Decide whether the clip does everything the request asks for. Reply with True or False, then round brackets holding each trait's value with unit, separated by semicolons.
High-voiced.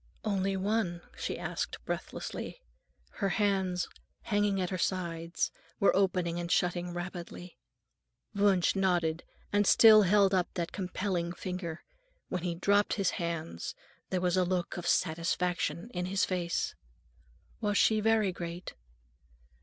False (180 Hz)